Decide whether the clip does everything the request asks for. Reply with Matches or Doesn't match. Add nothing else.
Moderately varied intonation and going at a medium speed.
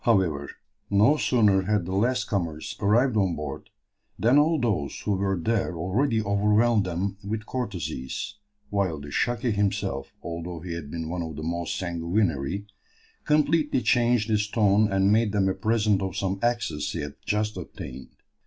Matches